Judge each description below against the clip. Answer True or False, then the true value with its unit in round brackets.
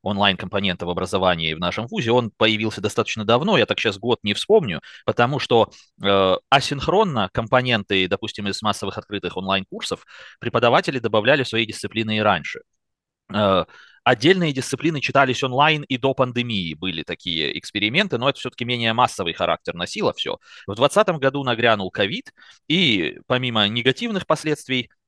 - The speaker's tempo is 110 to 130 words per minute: False (145 wpm)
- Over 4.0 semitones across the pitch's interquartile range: True (5.1 semitones)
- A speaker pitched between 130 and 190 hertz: False (115 Hz)